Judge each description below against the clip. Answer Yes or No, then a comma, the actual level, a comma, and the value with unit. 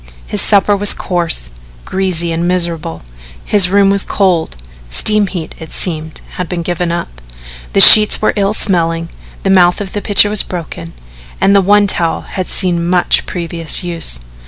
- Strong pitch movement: No, average, 2.9 semitones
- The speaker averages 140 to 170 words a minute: Yes, average, 165 wpm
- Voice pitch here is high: No, medium, 180 Hz